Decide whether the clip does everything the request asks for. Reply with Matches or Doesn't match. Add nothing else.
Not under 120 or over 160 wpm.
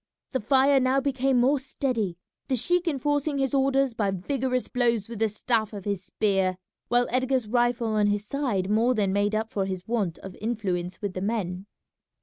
Doesn't match